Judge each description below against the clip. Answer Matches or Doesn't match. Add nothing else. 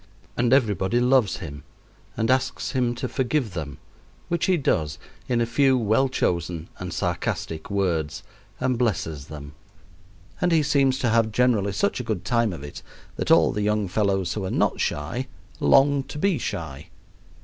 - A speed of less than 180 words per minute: Matches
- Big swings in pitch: Matches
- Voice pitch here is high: Doesn't match